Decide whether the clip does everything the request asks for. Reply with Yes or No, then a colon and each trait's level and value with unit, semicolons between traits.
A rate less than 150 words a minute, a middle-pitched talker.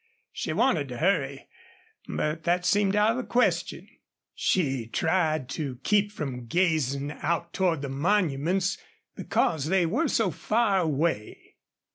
Yes: slow, 135 wpm; medium, 165 Hz